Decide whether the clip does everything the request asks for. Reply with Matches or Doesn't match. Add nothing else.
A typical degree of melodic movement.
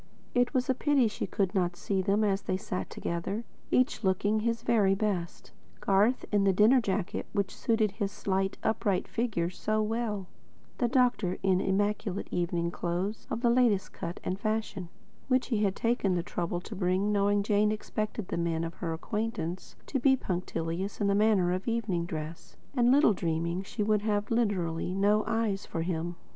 Matches